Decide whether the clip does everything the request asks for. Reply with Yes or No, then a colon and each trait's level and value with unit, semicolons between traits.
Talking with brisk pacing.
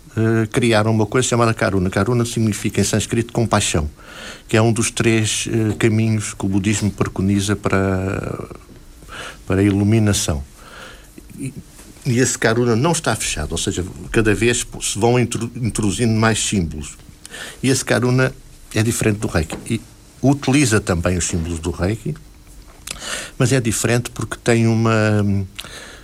No: average, 145 wpm